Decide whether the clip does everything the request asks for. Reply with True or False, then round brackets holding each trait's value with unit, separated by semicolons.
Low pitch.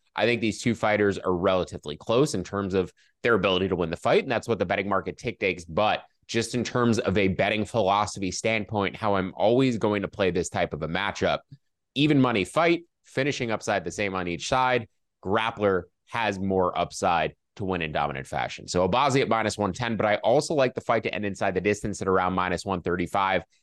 True (100 Hz)